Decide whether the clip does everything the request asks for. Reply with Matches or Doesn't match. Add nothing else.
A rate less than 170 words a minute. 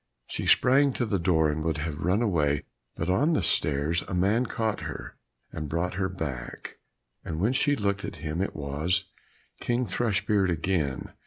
Doesn't match